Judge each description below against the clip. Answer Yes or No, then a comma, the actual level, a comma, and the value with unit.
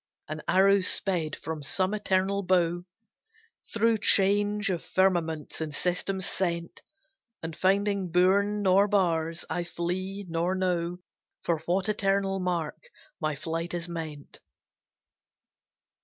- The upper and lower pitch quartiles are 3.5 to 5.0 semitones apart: No, average, 2.7 semitones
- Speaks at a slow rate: Yes, slow, 115 wpm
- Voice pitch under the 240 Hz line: Yes, medium, 185 Hz